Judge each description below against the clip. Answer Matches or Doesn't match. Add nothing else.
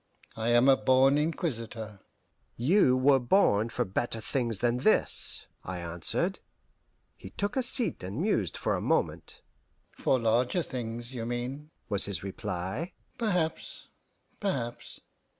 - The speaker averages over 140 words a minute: Doesn't match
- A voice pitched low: Matches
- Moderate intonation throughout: Matches